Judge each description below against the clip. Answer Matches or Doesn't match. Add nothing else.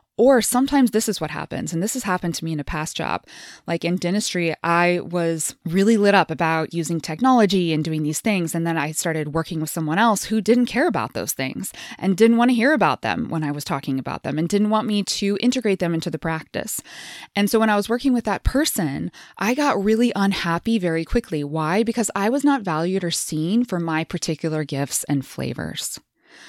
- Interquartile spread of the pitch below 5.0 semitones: Doesn't match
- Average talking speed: Doesn't match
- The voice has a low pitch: Doesn't match